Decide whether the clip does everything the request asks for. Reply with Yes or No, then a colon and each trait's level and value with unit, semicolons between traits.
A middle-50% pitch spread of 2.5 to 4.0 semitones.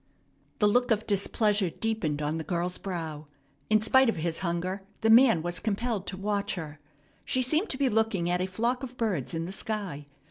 No: average, 4.6 semitones